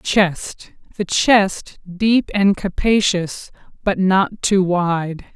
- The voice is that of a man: No, female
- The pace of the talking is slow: Yes, slow, 100 wpm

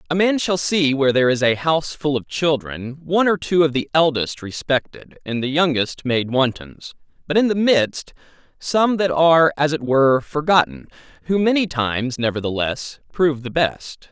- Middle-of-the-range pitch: Yes, medium, 145 Hz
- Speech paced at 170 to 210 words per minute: Yes, average, 180 wpm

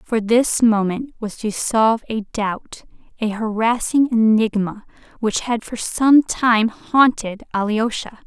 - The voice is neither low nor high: No, high, 225 Hz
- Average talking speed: No, slow, 130 wpm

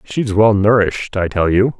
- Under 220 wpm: Yes, average, 200 wpm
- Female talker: No, male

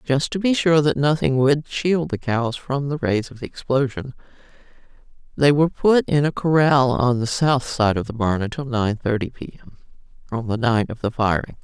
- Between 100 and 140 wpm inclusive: No, fast, 205 wpm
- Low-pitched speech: Yes, low, 130 Hz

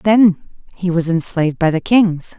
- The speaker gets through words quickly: No, average, 175 wpm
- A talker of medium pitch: Yes, medium, 180 Hz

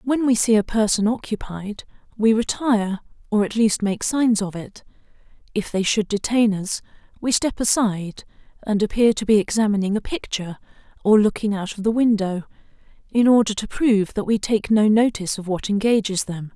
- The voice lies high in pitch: Yes, high, 210 Hz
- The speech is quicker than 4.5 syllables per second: Yes, 5.3 syllables/s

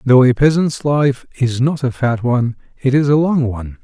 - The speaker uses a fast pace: Yes, fast, 220 wpm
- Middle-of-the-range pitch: No, low, 130 Hz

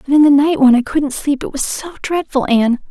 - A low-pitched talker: No, very high, 280 Hz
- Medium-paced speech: No, fast, 250 wpm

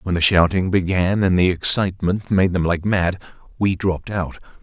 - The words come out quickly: No, average, 180 wpm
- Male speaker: Yes, male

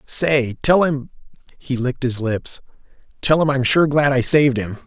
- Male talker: Yes, male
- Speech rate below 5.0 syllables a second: Yes, 4.7 syllables/s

